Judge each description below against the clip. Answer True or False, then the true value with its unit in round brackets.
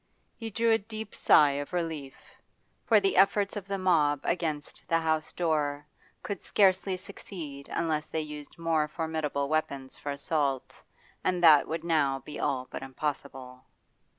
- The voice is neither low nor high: True (155 Hz)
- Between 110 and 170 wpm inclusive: True (150 wpm)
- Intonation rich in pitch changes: False (4.2 semitones)